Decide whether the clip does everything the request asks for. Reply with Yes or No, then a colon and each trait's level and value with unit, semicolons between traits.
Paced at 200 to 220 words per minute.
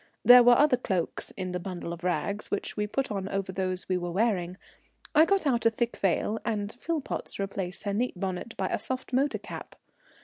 Yes: fast, 205 wpm